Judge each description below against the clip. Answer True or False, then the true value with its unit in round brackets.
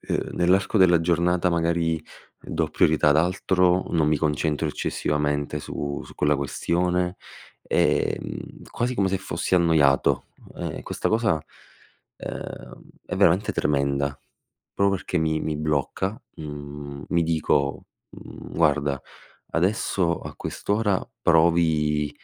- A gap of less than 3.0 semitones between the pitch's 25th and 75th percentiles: False (3.3 semitones)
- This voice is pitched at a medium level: False (80 Hz)